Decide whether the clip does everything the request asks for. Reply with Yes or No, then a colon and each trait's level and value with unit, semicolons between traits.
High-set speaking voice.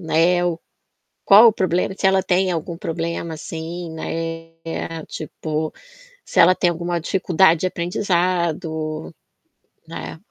No: medium, 170 Hz